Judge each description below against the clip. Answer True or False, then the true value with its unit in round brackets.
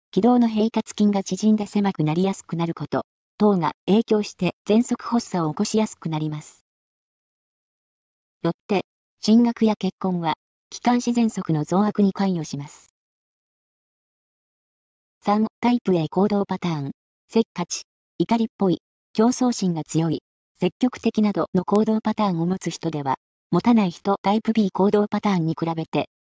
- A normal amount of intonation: True (4.3 semitones)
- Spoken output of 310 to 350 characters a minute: False (290 characters per minute)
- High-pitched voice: True (195 Hz)